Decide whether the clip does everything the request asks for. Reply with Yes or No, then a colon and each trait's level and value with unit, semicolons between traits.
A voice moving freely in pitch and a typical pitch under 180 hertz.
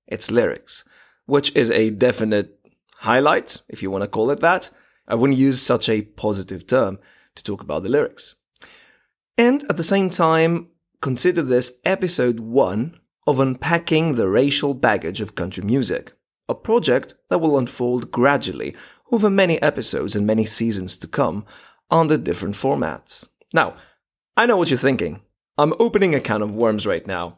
Yes: wide, 7.2 semitones; low, 135 Hz